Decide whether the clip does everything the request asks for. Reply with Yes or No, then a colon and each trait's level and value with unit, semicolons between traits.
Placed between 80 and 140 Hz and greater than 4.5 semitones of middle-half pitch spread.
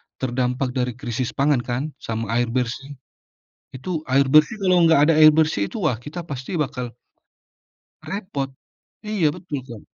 No: low, 135 Hz; average, 4.0 semitones